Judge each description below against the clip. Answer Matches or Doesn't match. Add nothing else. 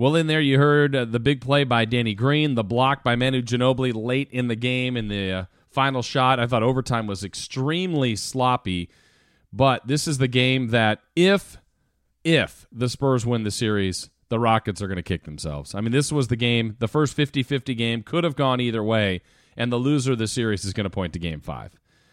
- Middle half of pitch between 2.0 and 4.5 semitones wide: Matches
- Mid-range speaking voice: Doesn't match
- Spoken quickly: Matches